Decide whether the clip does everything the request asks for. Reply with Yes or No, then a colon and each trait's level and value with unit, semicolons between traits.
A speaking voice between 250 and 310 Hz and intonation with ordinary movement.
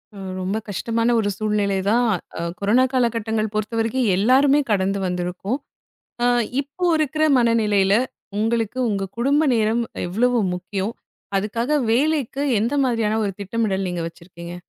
No: high, 220 Hz; average, 3.6 semitones